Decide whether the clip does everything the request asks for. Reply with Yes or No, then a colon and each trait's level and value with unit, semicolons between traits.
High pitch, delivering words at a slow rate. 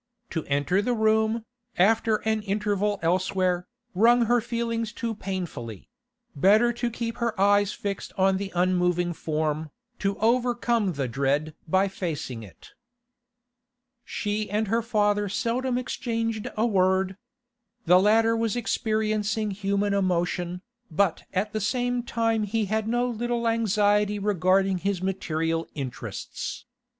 Yes: high, 205 Hz; slow, 130 wpm